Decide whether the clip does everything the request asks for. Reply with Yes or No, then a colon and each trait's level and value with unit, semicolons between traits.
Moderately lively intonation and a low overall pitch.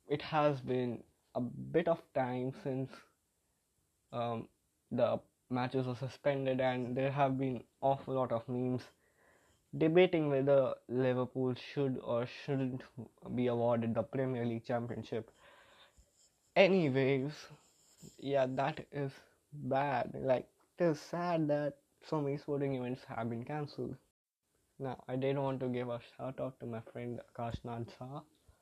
Yes: average, 3.0 semitones; low, 130 Hz